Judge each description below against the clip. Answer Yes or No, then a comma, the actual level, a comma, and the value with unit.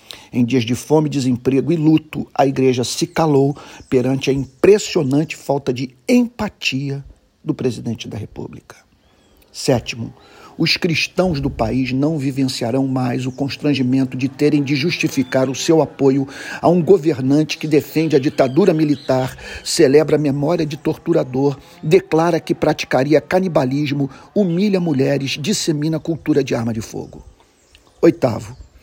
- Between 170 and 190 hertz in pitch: No, medium, 140 Hz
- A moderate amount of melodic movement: Yes, average, 3.3 semitones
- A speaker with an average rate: Yes, average, 135 wpm